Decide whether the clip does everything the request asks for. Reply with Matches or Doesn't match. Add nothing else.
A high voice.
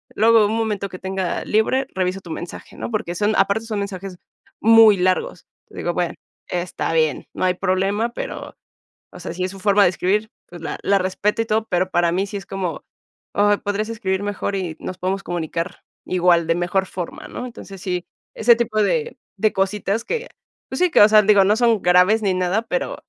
Matches